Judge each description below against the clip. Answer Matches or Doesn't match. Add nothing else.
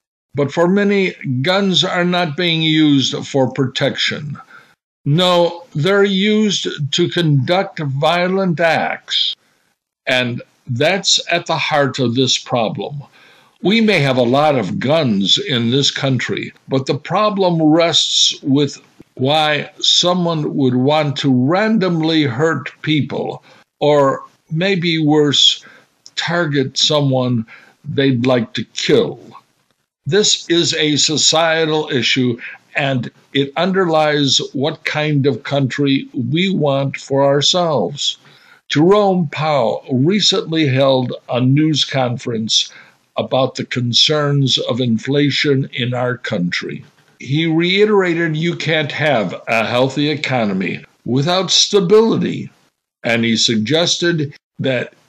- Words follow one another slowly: Matches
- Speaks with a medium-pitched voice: Matches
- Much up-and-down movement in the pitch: Doesn't match